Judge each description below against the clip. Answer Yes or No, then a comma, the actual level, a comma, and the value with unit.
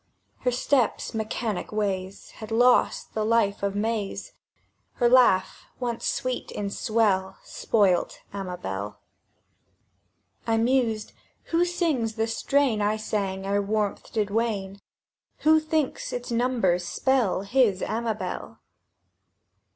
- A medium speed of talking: No, slow, 110 wpm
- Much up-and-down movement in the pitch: No, average, 3.5 semitones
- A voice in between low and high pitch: No, high, 220 Hz